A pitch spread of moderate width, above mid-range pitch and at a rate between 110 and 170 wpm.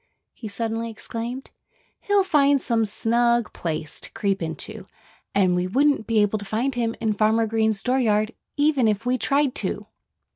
Yes: average, 3.2 semitones; high, 225 Hz; average, 160 wpm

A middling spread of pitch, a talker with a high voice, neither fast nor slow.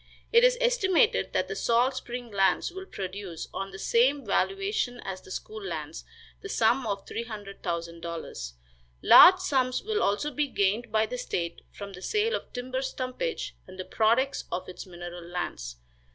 No: wide, 7.7 semitones; high, 235 Hz; average, 165 wpm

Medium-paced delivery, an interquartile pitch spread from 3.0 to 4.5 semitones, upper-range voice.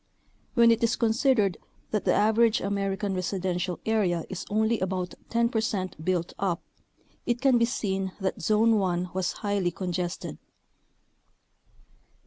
No: slow, 130 wpm; average, 3.4 semitones; high, 200 Hz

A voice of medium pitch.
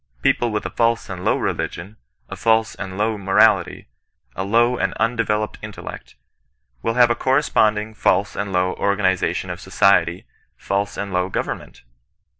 No: low, 100 Hz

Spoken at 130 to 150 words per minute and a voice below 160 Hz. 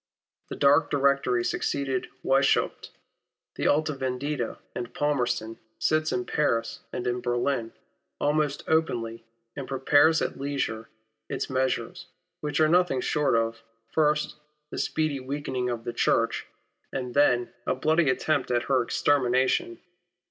Yes: average, 140 wpm; low, 135 Hz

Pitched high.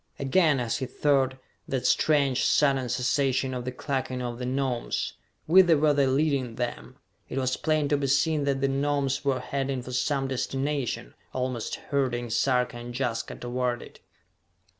No: low, 135 Hz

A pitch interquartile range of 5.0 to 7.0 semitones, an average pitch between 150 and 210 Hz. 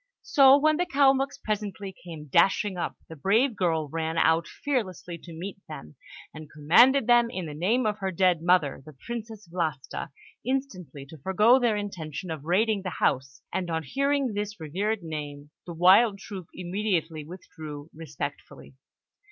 Yes: wide, 5.4 semitones; medium, 185 Hz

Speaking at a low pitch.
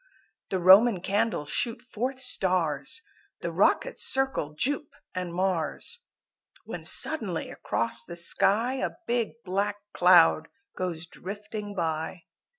No: high, 195 Hz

